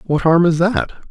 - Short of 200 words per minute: No, fast, 220 wpm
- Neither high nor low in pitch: Yes, medium, 165 Hz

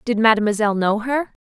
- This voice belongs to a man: No, female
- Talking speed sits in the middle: Yes, average, 165 wpm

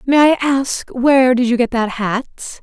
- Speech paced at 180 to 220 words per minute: Yes, fast, 205 wpm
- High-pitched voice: Yes, very high, 255 Hz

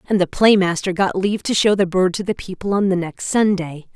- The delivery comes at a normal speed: No, fast, 260 wpm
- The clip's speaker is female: Yes, female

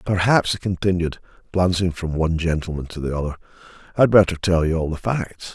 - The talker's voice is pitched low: Yes, very low, 90 Hz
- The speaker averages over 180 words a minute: Yes, average, 195 wpm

